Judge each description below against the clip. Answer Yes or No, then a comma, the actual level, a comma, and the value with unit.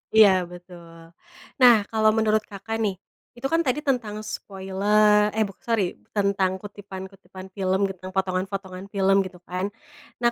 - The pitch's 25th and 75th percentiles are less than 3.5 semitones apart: Yes, narrow, 2.4 semitones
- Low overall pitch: No, high, 195 Hz